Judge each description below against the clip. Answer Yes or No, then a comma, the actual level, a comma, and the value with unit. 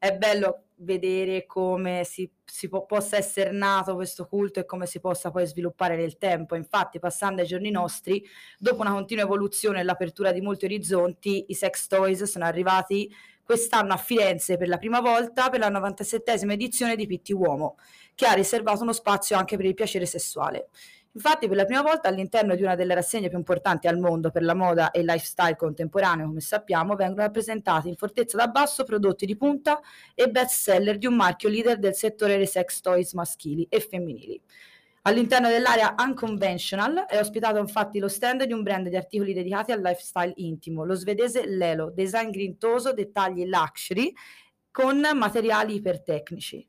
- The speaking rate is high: Yes, fast, 175 wpm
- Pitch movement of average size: Yes, average, 3.5 semitones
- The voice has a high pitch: Yes, high, 195 Hz